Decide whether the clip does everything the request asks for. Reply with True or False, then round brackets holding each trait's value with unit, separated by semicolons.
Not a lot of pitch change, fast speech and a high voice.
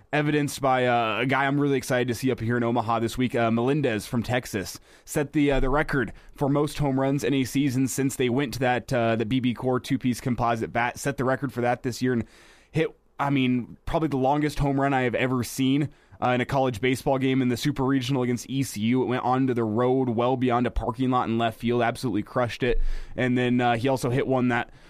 False (2.2 semitones; 240 wpm; 125 Hz)